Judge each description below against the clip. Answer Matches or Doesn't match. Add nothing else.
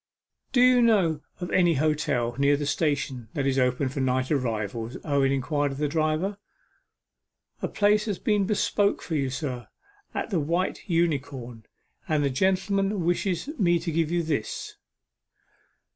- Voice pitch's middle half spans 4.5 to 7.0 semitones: Matches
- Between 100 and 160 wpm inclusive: Matches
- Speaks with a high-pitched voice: Doesn't match